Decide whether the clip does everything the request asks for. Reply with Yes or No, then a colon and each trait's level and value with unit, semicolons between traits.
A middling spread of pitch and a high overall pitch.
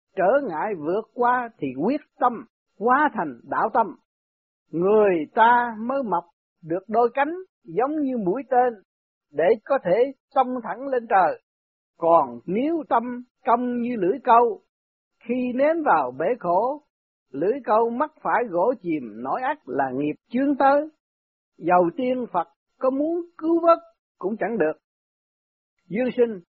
No: wide, 6.2 semitones; high, 245 Hz